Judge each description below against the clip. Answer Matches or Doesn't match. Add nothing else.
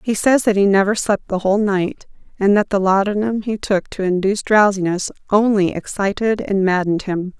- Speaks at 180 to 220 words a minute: Matches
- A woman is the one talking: Matches